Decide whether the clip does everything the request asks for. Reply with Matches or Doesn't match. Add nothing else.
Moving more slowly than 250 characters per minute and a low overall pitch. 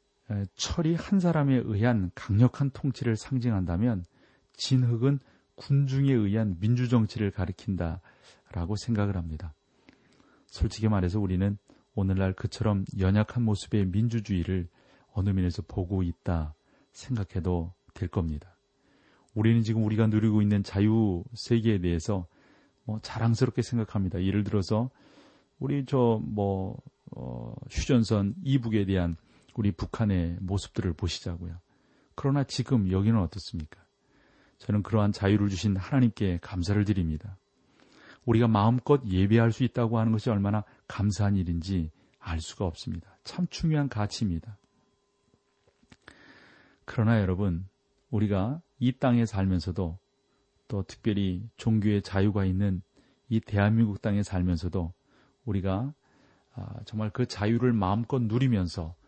Doesn't match